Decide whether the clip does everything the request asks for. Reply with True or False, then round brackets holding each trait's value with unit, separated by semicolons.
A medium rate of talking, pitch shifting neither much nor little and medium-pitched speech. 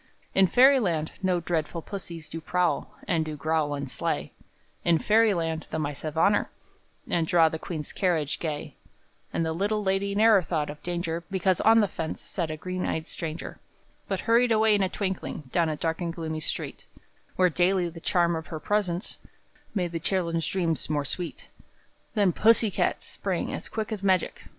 True (180 wpm; 3.3 semitones; 175 Hz)